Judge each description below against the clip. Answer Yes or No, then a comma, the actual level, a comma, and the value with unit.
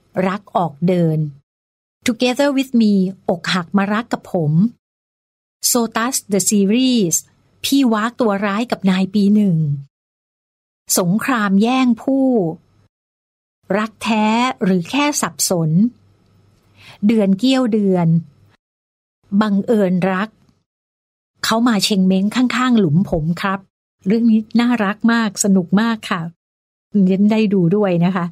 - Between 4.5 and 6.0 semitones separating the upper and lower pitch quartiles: Yes, average, 4.9 semitones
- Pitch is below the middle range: No, high, 200 Hz